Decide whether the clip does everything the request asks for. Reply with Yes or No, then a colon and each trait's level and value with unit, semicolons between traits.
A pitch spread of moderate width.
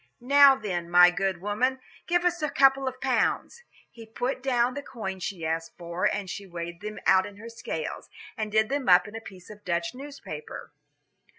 No: wide, 6.6 semitones